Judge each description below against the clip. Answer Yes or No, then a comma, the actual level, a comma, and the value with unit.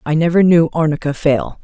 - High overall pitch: No, medium, 150 Hz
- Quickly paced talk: No, average, 185 wpm